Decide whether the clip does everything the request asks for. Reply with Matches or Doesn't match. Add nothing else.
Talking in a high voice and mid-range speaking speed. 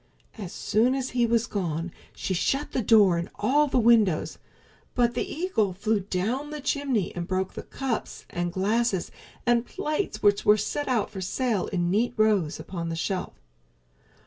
Matches